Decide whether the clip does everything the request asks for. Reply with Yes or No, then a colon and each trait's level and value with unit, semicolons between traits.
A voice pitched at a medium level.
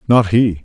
No: low, 105 Hz